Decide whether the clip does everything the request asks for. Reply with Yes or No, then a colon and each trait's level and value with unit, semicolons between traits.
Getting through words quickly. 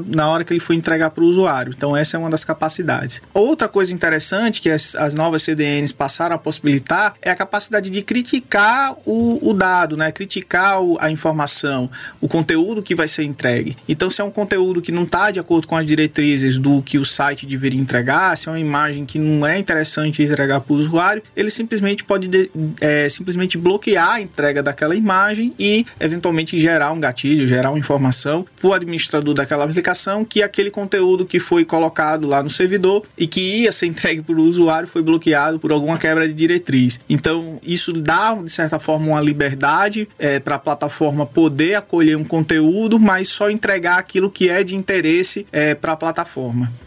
Yes: fast, 195 wpm